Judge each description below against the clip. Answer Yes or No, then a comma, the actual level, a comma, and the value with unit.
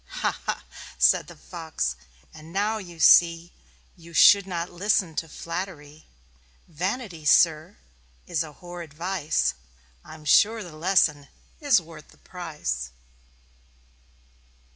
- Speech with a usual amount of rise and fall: Yes, average, 3.2 semitones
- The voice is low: No, medium, 170 Hz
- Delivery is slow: Yes, slow, 120 wpm